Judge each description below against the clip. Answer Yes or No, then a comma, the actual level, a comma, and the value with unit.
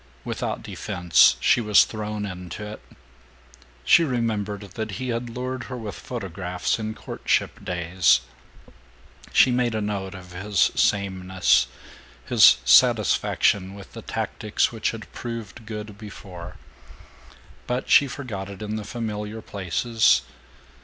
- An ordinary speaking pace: No, slow, 125 wpm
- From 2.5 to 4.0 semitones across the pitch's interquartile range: Yes, average, 3.5 semitones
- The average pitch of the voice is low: Yes, low, 105 Hz